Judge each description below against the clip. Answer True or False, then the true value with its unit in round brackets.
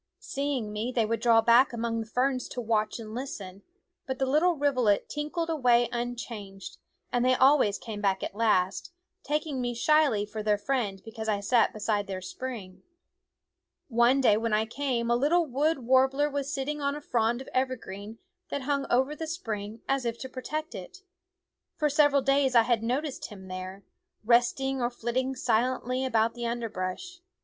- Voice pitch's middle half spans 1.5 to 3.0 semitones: False (3.8 semitones)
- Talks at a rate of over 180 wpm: False (175 wpm)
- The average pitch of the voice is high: True (245 Hz)